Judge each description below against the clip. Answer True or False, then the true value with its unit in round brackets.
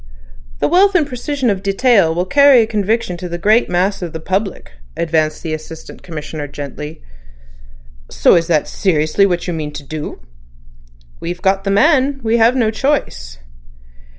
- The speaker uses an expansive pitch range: True (6.4 semitones)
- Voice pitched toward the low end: False (190 Hz)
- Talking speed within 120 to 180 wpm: True (160 wpm)